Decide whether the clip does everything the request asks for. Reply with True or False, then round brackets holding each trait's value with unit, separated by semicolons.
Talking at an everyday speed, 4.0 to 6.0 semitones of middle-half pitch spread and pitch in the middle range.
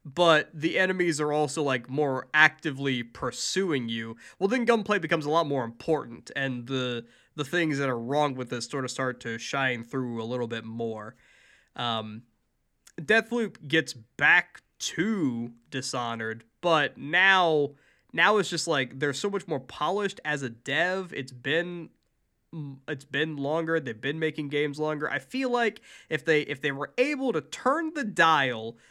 True (165 wpm; 4.8 semitones; 145 Hz)